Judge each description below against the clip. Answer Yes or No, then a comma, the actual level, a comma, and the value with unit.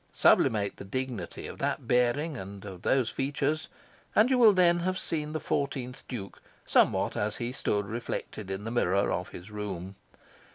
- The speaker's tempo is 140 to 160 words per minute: No, average, 170 wpm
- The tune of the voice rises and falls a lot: Yes, wide, 6.5 semitones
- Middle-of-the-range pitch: No, low, 120 Hz